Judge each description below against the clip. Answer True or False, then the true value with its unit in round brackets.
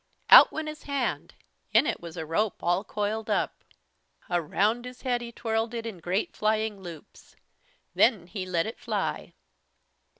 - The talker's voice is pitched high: True (215 Hz)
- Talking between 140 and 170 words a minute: True (160 wpm)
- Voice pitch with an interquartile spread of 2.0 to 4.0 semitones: False (4.8 semitones)